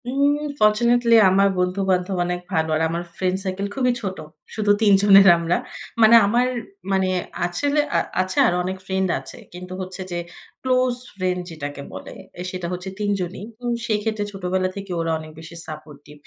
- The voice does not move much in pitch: No, average, 3.0 semitones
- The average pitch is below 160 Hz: No, high, 190 Hz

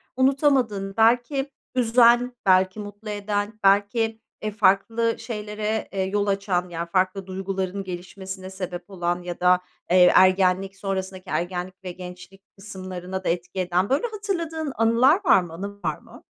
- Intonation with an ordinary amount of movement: Yes, average, 3.2 semitones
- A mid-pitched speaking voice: No, high, 195 Hz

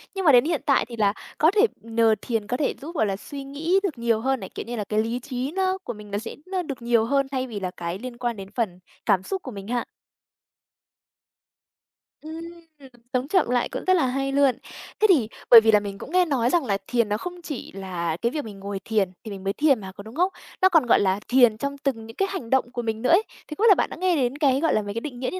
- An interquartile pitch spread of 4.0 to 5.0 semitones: No, wide, 5.6 semitones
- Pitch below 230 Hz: No, high, 245 Hz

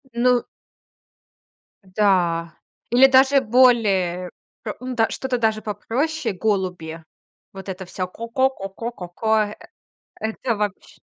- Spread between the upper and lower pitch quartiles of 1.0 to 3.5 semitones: No, average, 5.1 semitones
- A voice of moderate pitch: No, high, 215 Hz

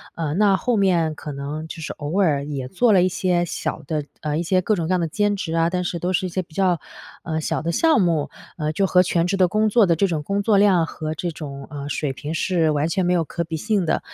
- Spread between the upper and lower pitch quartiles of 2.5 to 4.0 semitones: Yes, average, 3.4 semitones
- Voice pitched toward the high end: No, medium, 170 Hz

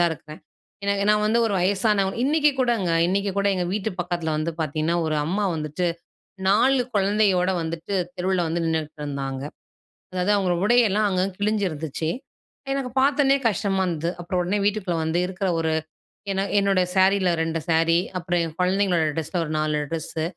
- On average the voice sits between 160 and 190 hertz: Yes, medium, 185 Hz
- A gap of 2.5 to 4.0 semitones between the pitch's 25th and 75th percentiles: Yes, average, 3.7 semitones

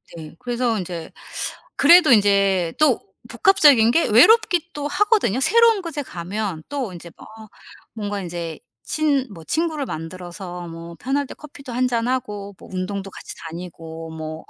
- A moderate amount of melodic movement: No, wide, 8.6 semitones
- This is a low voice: No, high, 215 Hz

